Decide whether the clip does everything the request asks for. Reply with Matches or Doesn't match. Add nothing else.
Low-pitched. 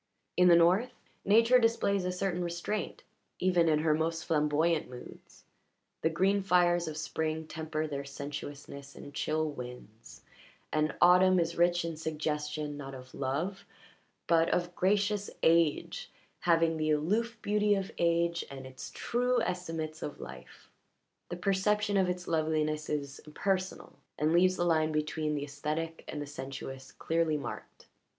Doesn't match